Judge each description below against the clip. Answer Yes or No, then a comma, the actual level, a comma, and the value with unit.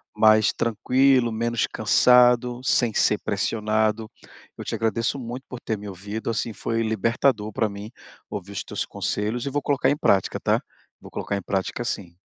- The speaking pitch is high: No, low, 110 Hz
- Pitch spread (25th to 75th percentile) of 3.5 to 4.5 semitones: No, average, 2.7 semitones